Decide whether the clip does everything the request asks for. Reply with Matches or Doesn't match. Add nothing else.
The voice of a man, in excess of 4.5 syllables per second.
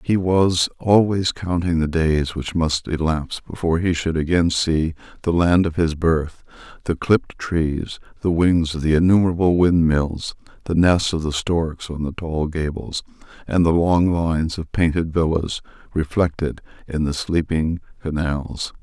Doesn't match